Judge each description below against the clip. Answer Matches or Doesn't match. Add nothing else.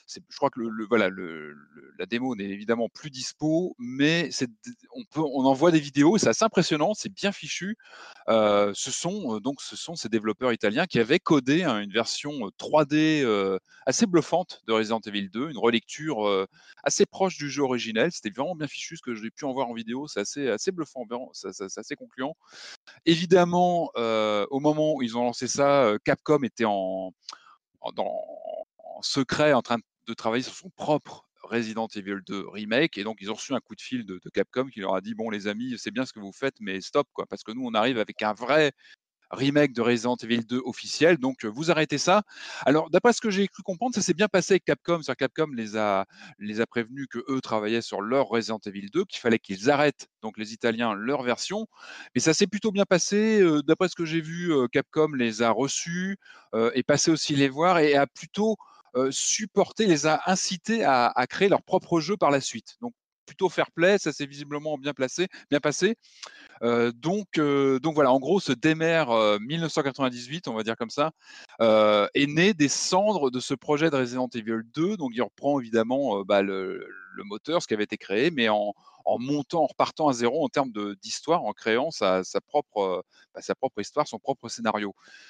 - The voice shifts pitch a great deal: Matches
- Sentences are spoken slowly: Doesn't match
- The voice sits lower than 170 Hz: Matches